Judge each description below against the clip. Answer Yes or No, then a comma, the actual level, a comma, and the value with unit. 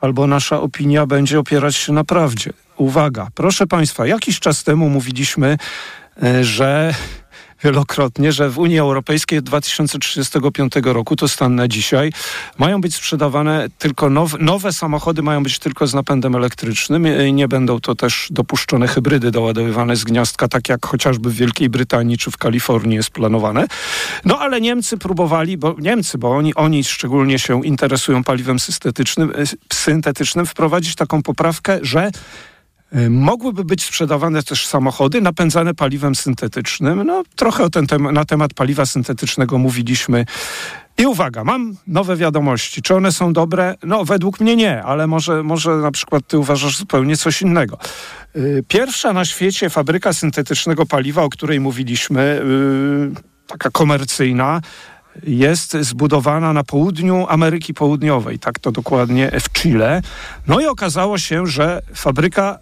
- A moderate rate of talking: Yes, average, 145 wpm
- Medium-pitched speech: Yes, medium, 150 Hz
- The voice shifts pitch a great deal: No, average, 3.7 semitones